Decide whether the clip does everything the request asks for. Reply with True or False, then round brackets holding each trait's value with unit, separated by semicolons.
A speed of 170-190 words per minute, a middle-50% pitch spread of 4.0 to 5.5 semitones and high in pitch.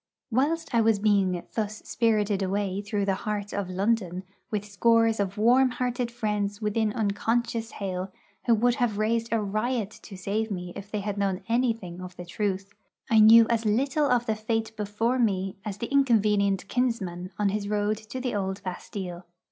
False (180 wpm; 2.6 semitones; 210 Hz)